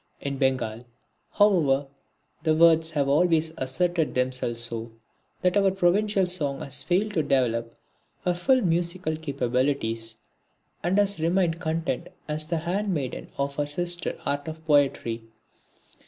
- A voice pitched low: No, medium, 155 Hz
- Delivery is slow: Yes, slow, 130 wpm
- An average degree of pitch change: Yes, average, 4.5 semitones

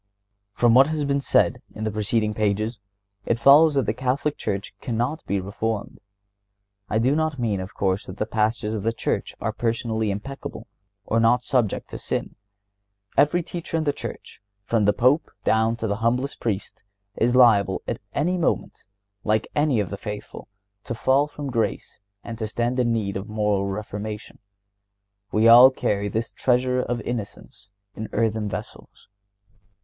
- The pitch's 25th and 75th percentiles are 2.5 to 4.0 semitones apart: Yes, average, 3.3 semitones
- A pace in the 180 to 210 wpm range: No, average, 165 wpm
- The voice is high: No, low, 115 Hz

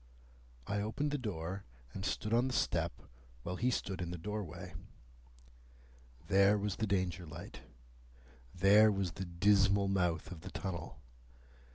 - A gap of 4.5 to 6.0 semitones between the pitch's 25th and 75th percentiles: No, average, 2.9 semitones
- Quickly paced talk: No, average, 145 wpm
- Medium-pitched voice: No, very low, 95 Hz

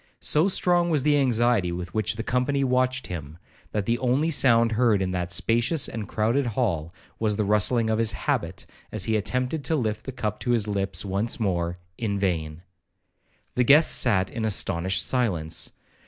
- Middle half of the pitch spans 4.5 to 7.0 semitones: Yes, average, 5.1 semitones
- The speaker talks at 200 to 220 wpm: No, average, 175 wpm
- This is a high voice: No, low, 110 Hz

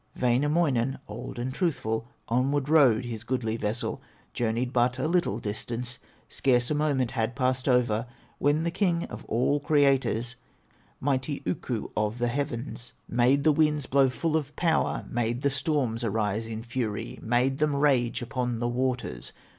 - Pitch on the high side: No, low, 125 Hz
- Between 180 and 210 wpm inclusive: No, average, 155 wpm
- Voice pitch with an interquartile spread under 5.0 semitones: Yes, average, 3.4 semitones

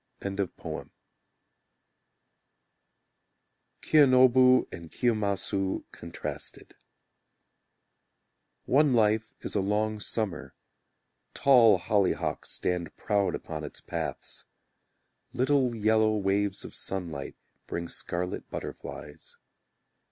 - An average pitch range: Yes, average, 4.9 semitones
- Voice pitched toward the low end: Yes, low, 105 Hz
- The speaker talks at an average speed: No, slow, 75 wpm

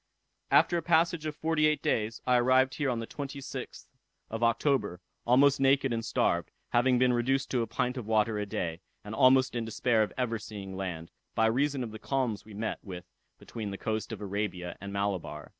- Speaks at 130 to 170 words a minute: No, average, 200 wpm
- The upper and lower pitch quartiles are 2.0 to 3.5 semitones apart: No, average, 4.2 semitones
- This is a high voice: No, low, 115 Hz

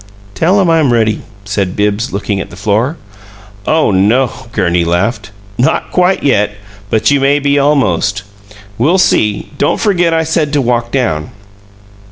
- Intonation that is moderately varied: No, wide, 6.5 semitones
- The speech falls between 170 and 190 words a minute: No, average, 155 wpm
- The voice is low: Yes, low, 120 Hz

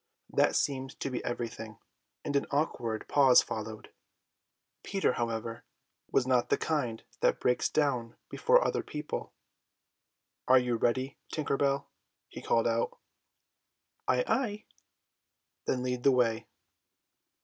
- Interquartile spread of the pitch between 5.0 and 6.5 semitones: No, average, 3.2 semitones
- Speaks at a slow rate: Yes, slow, 125 wpm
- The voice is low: Yes, low, 125 Hz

